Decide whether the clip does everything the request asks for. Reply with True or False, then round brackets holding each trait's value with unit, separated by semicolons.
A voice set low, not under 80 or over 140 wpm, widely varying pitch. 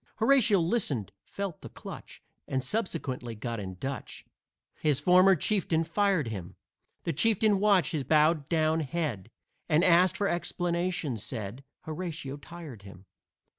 False (160 Hz; 135 wpm; 5.8 semitones)